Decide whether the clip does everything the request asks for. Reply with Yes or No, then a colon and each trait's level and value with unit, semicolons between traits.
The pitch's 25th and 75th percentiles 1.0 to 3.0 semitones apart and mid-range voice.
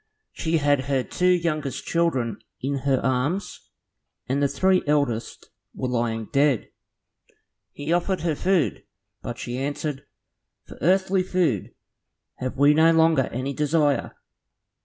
No: average, 4.2 semitones; medium, 145 Hz